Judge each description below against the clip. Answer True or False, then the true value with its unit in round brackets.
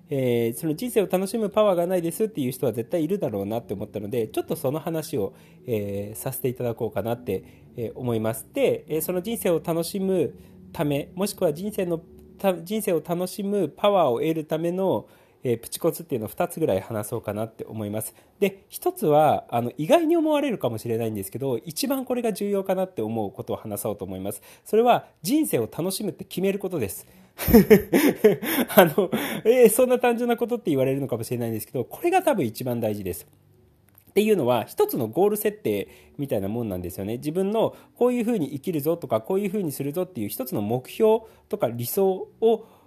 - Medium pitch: True (160 Hz)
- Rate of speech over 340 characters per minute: True (420 characters per minute)